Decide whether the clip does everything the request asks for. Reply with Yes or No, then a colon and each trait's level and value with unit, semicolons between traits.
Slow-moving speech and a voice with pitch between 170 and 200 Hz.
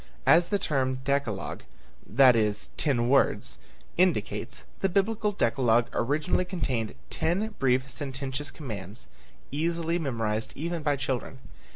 No: slow, 115 wpm; medium, 140 Hz